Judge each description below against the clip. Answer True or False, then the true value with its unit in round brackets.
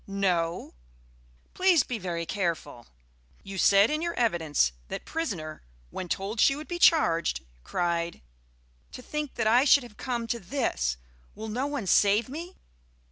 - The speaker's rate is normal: True (150 wpm)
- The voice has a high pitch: True (210 Hz)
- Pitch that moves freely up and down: True (8.1 semitones)